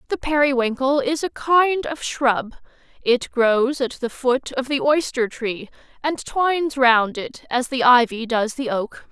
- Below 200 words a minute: Yes, average, 170 wpm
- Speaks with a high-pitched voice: Yes, very high, 260 Hz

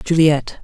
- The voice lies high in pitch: No, medium, 155 Hz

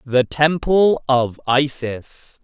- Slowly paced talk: Yes, slow, 100 wpm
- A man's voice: Yes, male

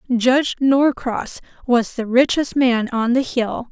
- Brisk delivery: No, average, 145 wpm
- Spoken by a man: No, female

